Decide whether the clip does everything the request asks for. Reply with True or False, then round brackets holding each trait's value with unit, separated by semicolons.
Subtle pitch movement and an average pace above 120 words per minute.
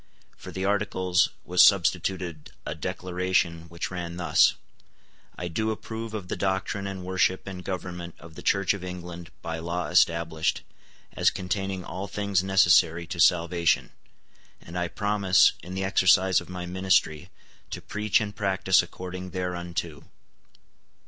True (1.9 semitones; 140 wpm)